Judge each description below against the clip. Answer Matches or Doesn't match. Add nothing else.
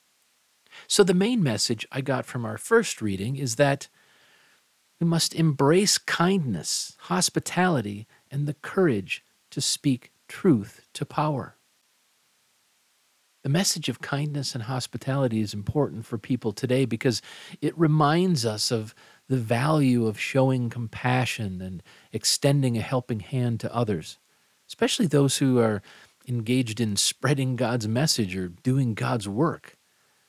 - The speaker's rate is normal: Doesn't match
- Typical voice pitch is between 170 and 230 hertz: Doesn't match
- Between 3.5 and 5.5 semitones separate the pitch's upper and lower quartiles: Matches